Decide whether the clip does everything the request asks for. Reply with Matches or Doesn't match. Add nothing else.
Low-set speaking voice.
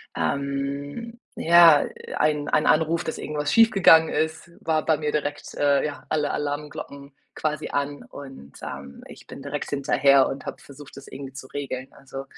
Doesn't match